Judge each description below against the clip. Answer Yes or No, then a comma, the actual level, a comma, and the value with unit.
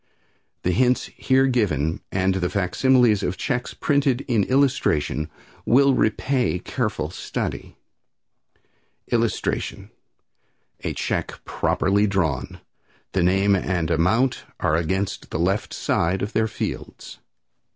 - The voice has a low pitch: Yes, low, 100 Hz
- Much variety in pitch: Yes, wide, 5.9 semitones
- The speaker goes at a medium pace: No, slow, 110 wpm